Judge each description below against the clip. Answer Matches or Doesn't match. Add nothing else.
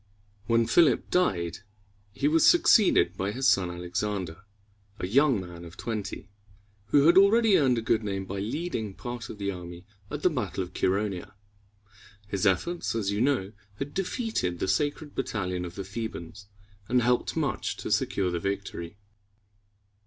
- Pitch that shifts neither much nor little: Doesn't match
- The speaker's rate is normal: Matches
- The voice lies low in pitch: Matches